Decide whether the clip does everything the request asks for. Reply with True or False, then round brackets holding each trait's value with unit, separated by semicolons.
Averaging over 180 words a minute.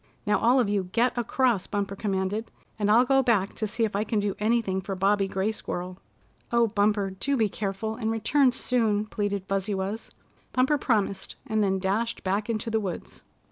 True (190 wpm)